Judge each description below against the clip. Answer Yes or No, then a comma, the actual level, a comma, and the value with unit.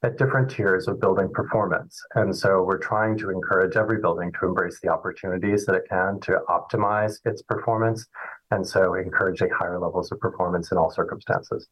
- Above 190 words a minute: No, average, 180 wpm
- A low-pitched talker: Yes, low, 110 Hz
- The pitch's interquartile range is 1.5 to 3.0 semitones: Yes, average, 2.7 semitones